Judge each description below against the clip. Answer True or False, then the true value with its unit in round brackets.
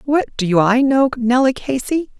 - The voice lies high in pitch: True (255 Hz)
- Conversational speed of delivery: True (165 wpm)